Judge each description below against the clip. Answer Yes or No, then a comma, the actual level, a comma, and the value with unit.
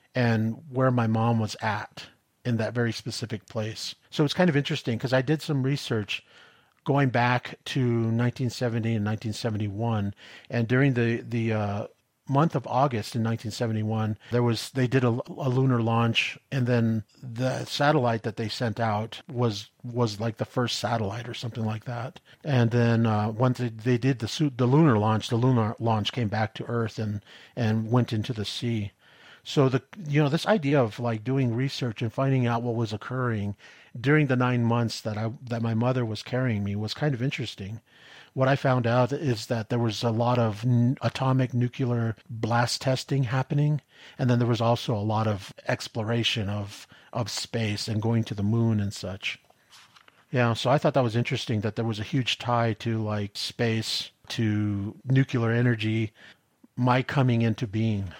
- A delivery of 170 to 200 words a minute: Yes, average, 185 wpm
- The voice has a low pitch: Yes, low, 120 Hz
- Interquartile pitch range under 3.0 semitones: Yes, narrow, 2.6 semitones